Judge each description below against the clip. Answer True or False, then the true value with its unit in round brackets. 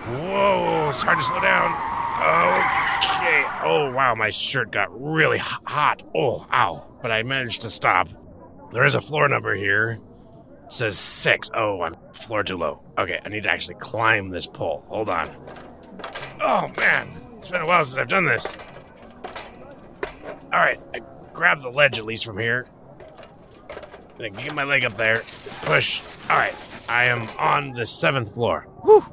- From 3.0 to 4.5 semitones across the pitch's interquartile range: True (3.6 semitones)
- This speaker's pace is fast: False (165 wpm)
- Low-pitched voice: True (115 Hz)